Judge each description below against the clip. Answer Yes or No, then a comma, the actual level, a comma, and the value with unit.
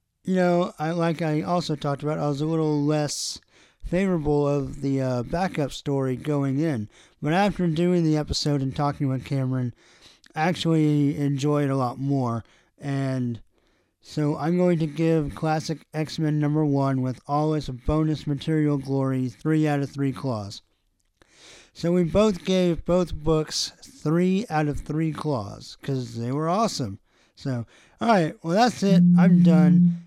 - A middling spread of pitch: Yes, average, 3.5 semitones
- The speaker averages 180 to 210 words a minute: No, average, 160 wpm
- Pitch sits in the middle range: Yes, medium, 150 Hz